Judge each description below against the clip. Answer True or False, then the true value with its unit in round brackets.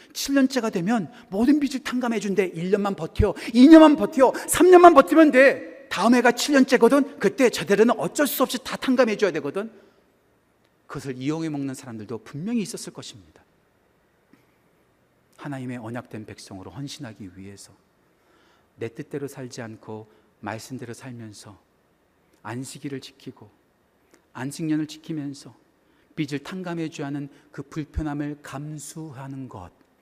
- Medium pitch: True (150 Hz)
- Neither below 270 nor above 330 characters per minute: True (290 characters per minute)